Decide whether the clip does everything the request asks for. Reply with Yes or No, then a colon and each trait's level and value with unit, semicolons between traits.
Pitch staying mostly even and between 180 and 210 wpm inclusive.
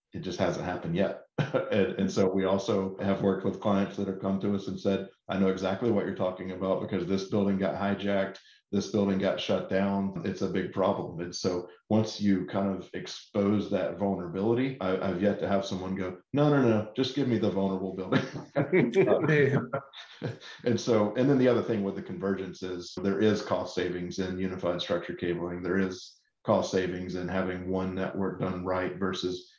Yes: narrow, 1.4 semitones; average, 200 wpm